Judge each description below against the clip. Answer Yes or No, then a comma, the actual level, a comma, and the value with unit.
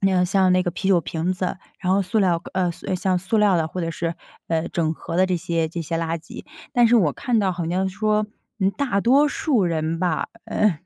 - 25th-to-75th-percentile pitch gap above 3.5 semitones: No, average, 3.0 semitones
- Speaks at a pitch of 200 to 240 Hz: No, medium, 185 Hz